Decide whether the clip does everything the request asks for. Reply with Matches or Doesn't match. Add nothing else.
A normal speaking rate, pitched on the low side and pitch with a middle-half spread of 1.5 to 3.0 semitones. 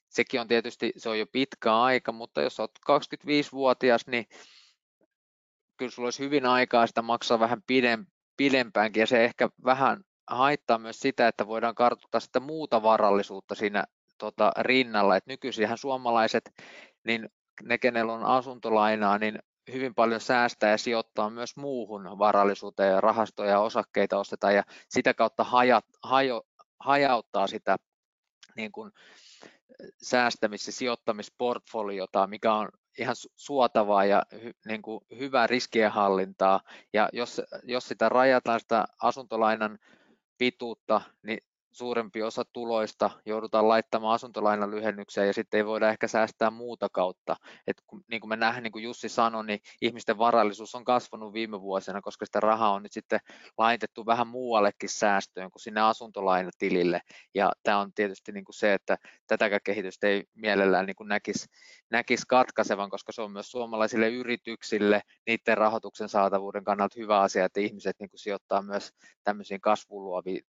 Matches